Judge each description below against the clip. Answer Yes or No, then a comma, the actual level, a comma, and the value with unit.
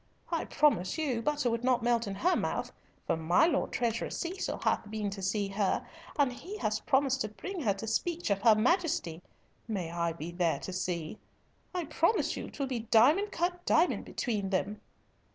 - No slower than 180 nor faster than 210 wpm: Yes, average, 190 wpm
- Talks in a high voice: Yes, high, 230 Hz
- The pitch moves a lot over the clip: Yes, wide, 7.4 semitones